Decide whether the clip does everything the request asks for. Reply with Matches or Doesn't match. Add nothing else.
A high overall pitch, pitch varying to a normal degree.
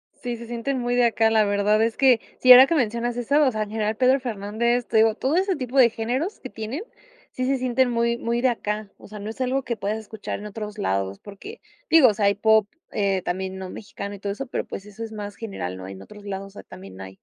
Matches